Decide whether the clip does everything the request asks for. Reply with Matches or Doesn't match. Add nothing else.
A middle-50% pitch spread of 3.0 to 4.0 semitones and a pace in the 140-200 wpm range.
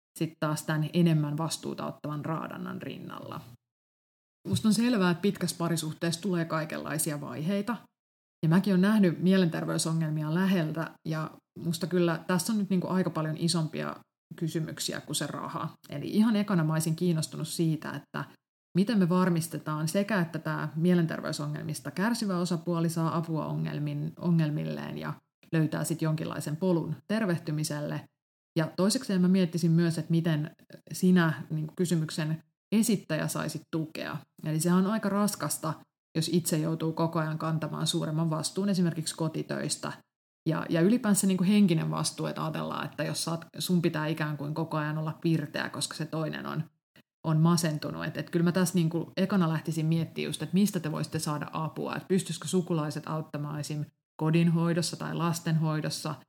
Doesn't match